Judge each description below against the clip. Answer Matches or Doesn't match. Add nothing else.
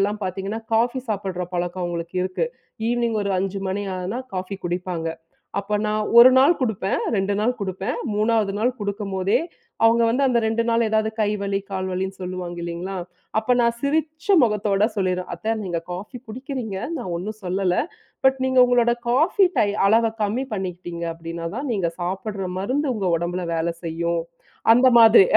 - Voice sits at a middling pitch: Doesn't match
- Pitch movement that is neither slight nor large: Matches